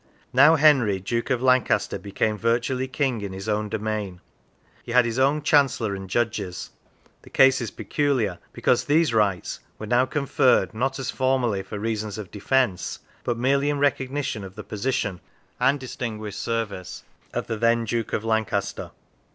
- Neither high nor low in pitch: No, low, 115 Hz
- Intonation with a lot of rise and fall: No, average, 4.0 semitones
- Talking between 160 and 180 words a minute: Yes, average, 165 wpm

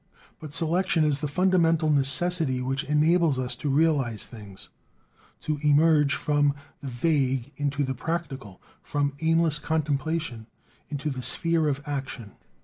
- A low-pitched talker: No, medium, 145 Hz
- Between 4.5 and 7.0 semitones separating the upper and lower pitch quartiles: No, average, 3.2 semitones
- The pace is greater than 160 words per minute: No, slow, 135 wpm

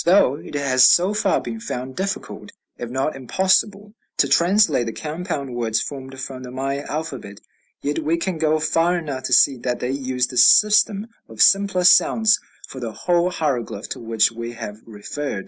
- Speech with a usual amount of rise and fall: No, wide, 6.1 semitones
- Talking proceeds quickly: No, average, 180 wpm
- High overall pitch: No, medium, 140 Hz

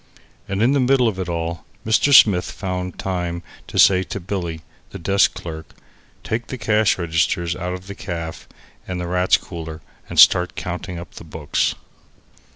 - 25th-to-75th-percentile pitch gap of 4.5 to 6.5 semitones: No, average, 2.8 semitones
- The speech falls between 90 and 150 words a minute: No, average, 170 wpm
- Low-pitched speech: Yes, very low, 90 Hz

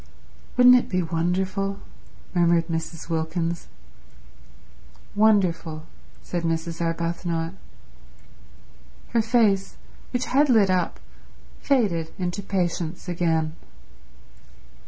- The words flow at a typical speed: No, slow, 85 wpm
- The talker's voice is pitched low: No, medium, 175 Hz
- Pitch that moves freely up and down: No, average, 3.1 semitones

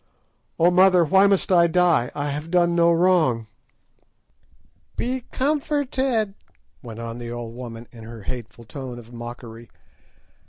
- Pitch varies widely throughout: Yes, wide, 7.7 semitones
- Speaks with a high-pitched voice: No, medium, 150 Hz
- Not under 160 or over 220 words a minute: No, slow, 135 wpm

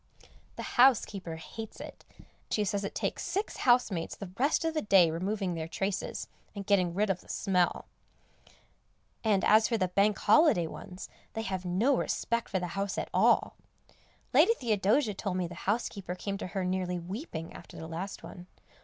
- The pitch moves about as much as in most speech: Yes, average, 3.3 semitones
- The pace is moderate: Yes, average, 175 wpm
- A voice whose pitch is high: Yes, high, 195 Hz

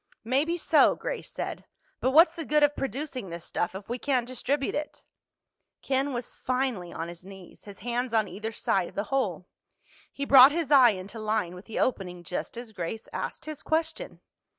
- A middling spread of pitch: No, wide, 6.3 semitones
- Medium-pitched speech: No, high, 245 Hz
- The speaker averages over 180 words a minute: Yes, average, 190 wpm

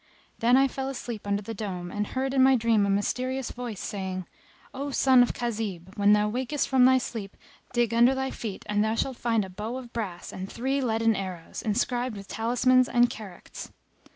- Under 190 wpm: No, average, 200 wpm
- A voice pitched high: Yes, high, 230 Hz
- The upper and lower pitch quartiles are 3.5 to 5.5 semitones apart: Yes, average, 3.8 semitones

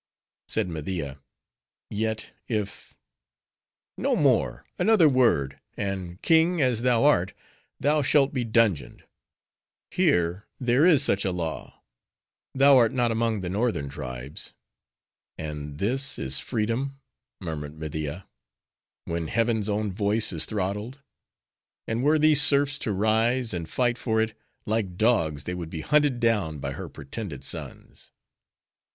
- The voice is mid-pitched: No, low, 110 Hz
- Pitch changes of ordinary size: No, wide, 6.7 semitones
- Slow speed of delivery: Yes, slow, 130 wpm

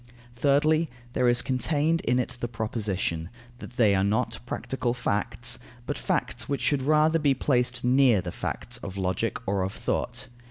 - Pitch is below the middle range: Yes, low, 125 Hz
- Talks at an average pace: Yes, average, 165 wpm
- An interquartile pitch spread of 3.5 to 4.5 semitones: No, average, 5.1 semitones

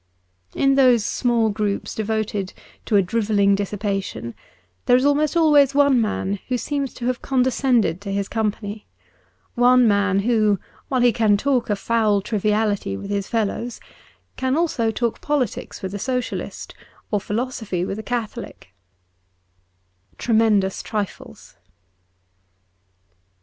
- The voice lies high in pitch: Yes, high, 220 Hz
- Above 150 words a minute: No, slow, 135 wpm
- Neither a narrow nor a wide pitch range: Yes, average, 3.7 semitones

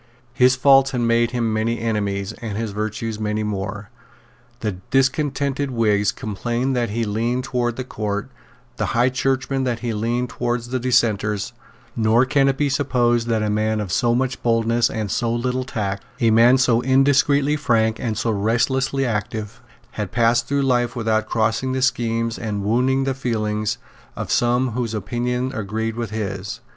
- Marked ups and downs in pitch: No, average, 2.8 semitones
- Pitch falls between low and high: No, low, 115 Hz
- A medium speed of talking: Yes, average, 170 wpm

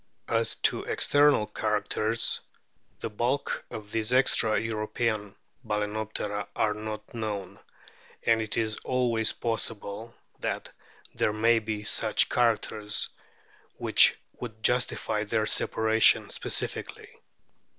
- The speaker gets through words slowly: Yes, slow, 105 wpm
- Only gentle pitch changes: Yes, narrow, 1.4 semitones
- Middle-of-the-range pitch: No, low, 110 Hz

